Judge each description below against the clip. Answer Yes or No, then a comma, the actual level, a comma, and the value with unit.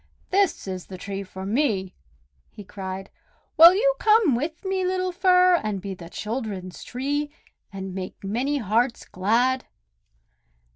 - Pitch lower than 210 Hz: No, high, 235 Hz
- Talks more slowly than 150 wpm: Yes, average, 140 wpm